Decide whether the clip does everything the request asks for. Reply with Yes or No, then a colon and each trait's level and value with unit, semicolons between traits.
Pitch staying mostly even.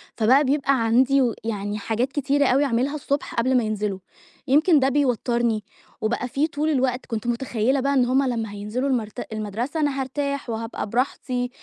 No: average, 3.4 semitones